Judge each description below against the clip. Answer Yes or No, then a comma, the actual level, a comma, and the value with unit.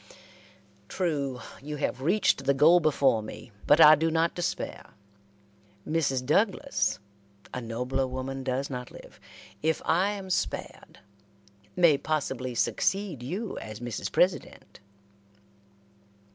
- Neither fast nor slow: No, slow, 115 wpm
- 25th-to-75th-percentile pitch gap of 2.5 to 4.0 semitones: No, average, 4.8 semitones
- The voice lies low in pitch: No, medium, 145 Hz